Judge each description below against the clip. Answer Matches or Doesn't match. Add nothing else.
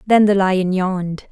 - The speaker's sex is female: Matches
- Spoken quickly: Doesn't match